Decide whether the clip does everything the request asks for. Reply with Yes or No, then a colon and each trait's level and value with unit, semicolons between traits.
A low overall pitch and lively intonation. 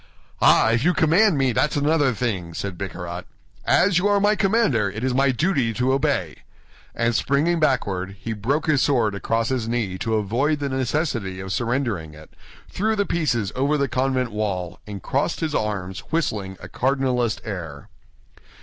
Yes: low, 125 Hz; wide, 6.1 semitones